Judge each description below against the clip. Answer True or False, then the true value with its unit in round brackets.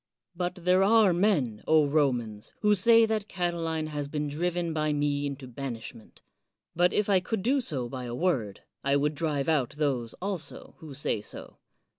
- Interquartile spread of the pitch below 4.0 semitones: False (4.7 semitones)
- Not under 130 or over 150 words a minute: False (170 wpm)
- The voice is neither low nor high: True (155 Hz)